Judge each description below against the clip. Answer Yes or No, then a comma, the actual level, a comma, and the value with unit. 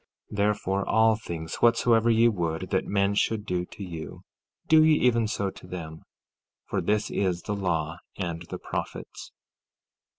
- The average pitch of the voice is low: Yes, low, 100 Hz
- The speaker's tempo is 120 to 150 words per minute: No, average, 160 wpm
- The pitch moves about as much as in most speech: Yes, average, 4.4 semitones